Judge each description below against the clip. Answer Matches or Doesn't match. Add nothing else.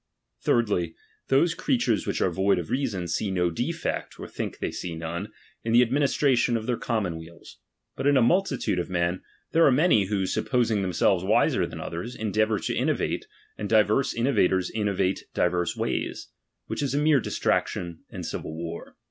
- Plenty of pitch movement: Matches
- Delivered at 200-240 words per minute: Doesn't match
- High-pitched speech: Doesn't match